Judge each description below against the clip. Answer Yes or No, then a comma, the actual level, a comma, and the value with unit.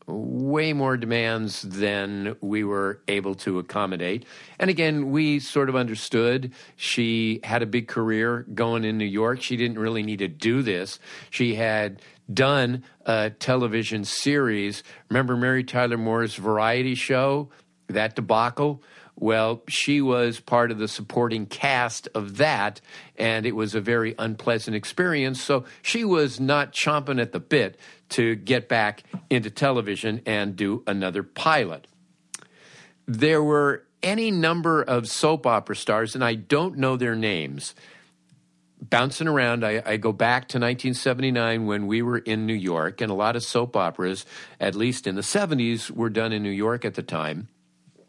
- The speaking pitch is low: Yes, low, 115 Hz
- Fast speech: No, average, 155 wpm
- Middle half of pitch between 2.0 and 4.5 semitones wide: Yes, average, 3.4 semitones